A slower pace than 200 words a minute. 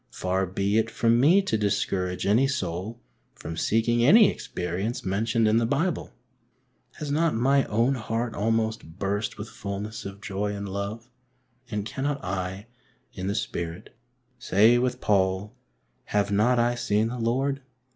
Yes: average, 150 wpm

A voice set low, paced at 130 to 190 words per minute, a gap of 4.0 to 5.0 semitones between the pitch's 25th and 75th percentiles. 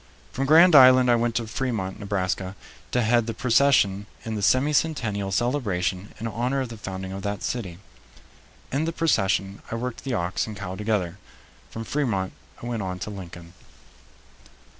Yes: low, 110 Hz; average, 170 wpm; average, 4.7 semitones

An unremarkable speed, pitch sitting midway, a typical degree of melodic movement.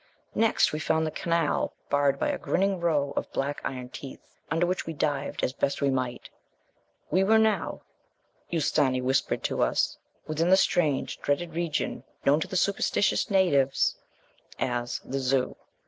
Yes: average, 165 wpm; medium, 150 Hz; average, 4.2 semitones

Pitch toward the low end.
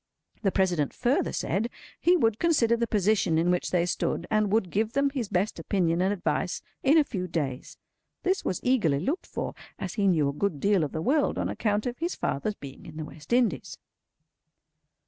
No: high, 200 Hz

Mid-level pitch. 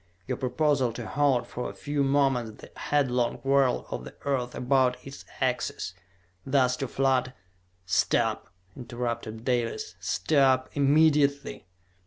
No: low, 130 Hz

